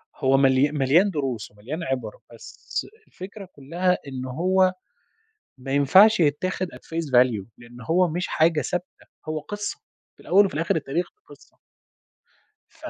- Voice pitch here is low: No, medium, 155 Hz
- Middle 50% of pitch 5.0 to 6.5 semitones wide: Yes, wide, 5.4 semitones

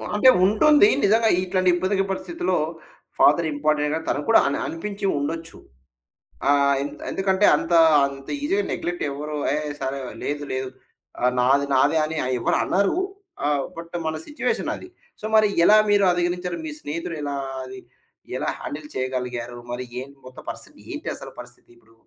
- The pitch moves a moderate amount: No, wide, 5.8 semitones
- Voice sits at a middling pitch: Yes, medium, 155 Hz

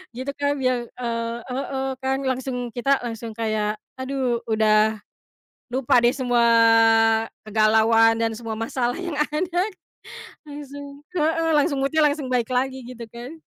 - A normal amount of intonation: Yes, average, 3.4 semitones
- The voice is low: No, very high, 250 Hz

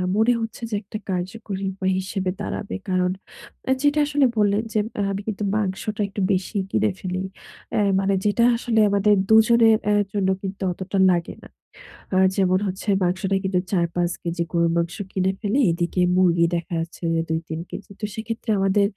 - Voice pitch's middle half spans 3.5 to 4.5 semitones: No, average, 2.9 semitones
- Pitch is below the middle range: No, high, 195 Hz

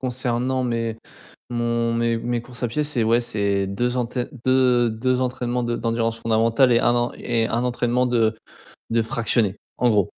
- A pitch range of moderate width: No, narrow, 1.5 semitones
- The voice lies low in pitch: Yes, low, 120 Hz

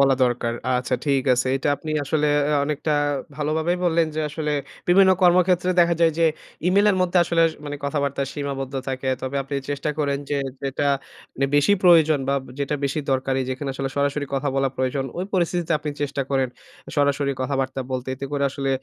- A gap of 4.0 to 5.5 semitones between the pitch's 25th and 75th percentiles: No, average, 2.8 semitones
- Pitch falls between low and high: Yes, medium, 145 Hz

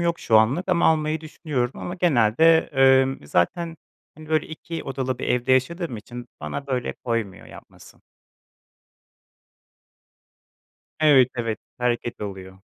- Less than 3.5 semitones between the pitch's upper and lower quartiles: No, wide, 5.5 semitones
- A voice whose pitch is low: Yes, low, 130 Hz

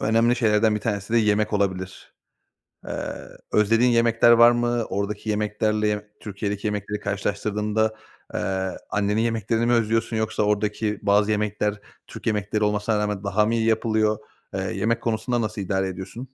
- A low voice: Yes, low, 105 Hz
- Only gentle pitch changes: Yes, narrow, 1.6 semitones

